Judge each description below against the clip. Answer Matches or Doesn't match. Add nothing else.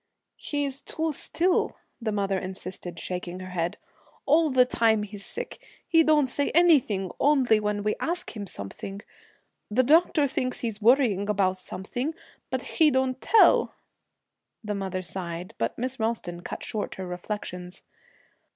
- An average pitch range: Doesn't match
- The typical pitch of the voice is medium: Doesn't match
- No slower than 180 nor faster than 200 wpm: Doesn't match